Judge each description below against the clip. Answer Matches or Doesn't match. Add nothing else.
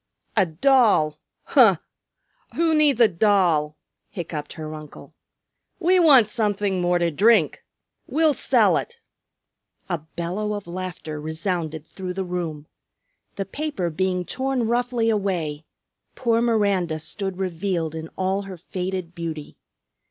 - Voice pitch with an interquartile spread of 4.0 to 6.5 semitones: Matches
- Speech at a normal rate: Doesn't match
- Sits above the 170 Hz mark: Matches